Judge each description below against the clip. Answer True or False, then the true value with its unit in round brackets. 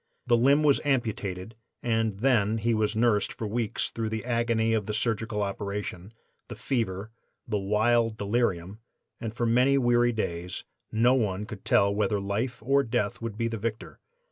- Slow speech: False (170 wpm)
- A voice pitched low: True (110 Hz)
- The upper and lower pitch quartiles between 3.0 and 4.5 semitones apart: False (2.5 semitones)